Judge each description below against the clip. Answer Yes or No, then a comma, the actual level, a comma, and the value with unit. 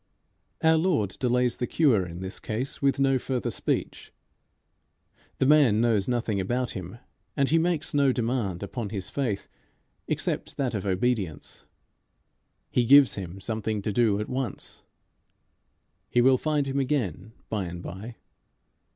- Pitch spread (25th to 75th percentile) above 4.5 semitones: Yes, average, 5.1 semitones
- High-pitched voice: No, low, 120 Hz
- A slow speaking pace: No, average, 145 wpm